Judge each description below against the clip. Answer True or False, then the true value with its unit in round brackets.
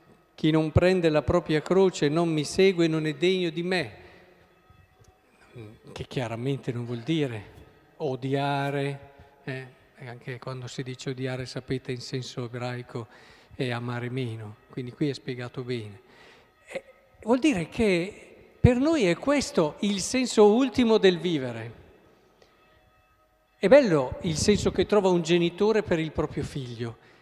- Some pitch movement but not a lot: False (6.5 semitones)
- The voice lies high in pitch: False (140 Hz)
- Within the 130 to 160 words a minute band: True (135 wpm)